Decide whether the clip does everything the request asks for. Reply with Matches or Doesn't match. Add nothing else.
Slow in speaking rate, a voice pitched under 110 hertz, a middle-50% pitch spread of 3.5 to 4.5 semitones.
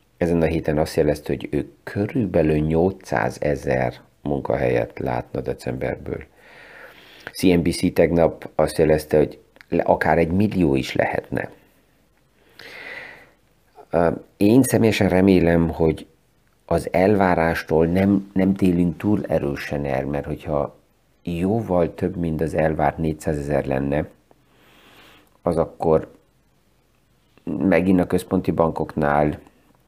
Matches